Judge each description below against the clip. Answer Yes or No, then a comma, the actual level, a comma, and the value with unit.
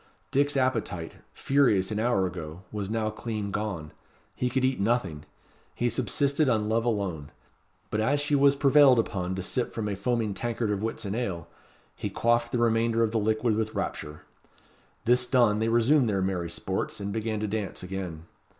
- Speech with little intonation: No, average, 3.7 semitones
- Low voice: Yes, low, 110 Hz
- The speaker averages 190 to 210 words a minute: No, average, 175 wpm